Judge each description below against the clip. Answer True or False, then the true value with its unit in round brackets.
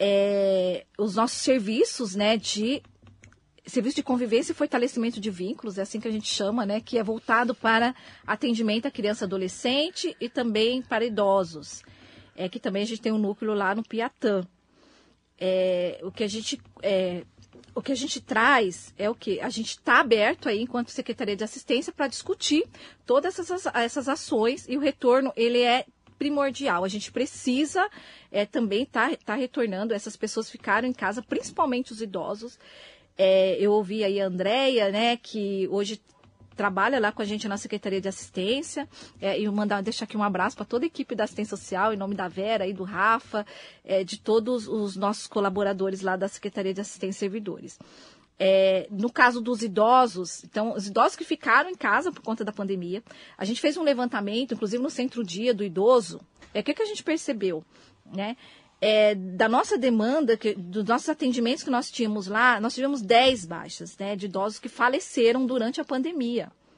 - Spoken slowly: False (185 wpm)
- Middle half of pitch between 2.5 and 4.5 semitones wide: True (4.0 semitones)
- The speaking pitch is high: True (225 Hz)